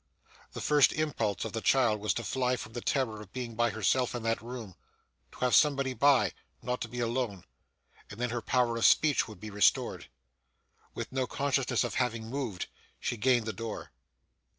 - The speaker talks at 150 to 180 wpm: No, average, 190 wpm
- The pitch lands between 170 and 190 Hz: No, low, 120 Hz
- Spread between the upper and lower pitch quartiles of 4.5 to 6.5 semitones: No, average, 2.7 semitones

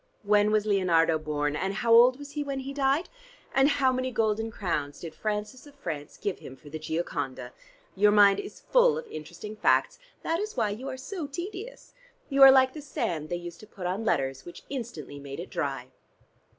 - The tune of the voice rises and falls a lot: Yes, wide, 8.6 semitones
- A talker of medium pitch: No, high, 210 Hz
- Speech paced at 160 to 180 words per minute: No, fast, 205 wpm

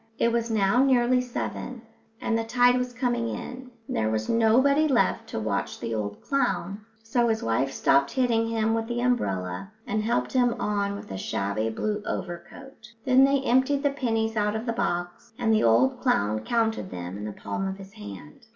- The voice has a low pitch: No, high, 225 Hz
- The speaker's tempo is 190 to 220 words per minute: Yes, average, 195 wpm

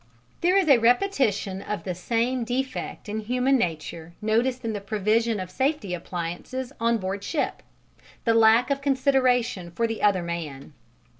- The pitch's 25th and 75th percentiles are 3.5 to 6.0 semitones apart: Yes, average, 5.2 semitones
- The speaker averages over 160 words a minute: No, average, 155 wpm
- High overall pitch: Yes, high, 225 Hz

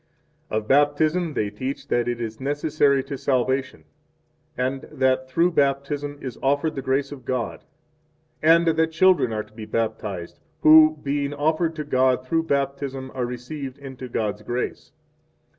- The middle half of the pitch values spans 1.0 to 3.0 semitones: Yes, average, 2.7 semitones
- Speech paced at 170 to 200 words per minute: No, average, 160 wpm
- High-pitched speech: No, low, 135 Hz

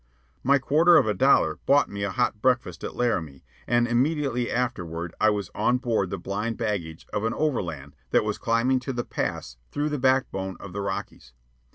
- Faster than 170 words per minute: Yes, average, 190 wpm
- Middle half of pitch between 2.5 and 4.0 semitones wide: No, average, 5.3 semitones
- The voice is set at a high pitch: No, low, 115 Hz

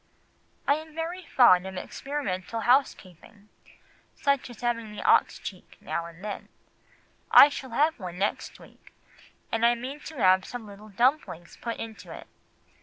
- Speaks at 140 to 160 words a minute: Yes, average, 155 wpm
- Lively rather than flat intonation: Yes, wide, 6.5 semitones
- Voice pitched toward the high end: Yes, high, 230 Hz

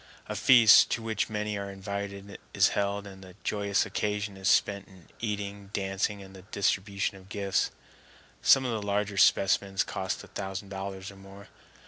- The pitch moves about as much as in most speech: No, narrow, 1.1 semitones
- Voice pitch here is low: Yes, low, 100 Hz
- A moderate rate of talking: Yes, average, 170 wpm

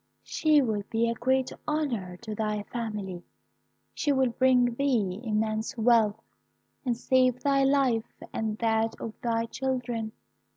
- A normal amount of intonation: Yes, average, 3.1 semitones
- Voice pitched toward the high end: Yes, high, 230 Hz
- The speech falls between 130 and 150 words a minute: Yes, average, 140 wpm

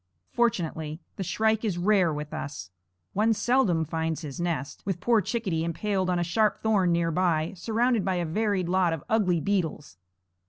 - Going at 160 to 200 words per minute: Yes, average, 170 wpm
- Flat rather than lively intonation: No, average, 4.6 semitones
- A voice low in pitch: No, medium, 180 Hz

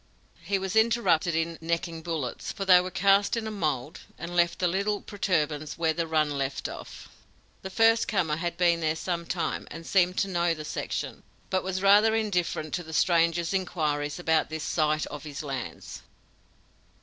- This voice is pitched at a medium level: Yes, medium, 170 Hz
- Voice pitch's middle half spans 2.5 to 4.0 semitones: Yes, average, 3.3 semitones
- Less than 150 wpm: No, average, 180 wpm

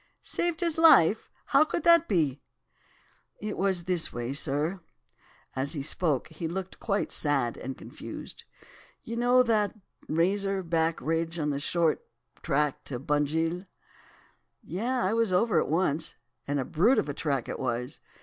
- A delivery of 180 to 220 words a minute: No, average, 155 wpm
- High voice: No, medium, 165 Hz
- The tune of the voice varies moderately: No, wide, 5.9 semitones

